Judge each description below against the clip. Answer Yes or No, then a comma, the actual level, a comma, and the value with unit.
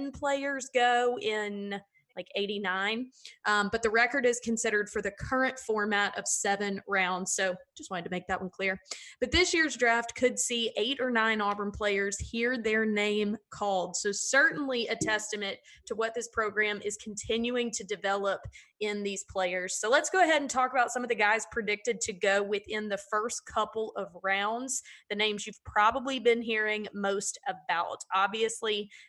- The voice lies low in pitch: No, high, 215 Hz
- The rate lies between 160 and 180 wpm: Yes, average, 175 wpm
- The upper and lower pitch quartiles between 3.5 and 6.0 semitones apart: No, average, 3.0 semitones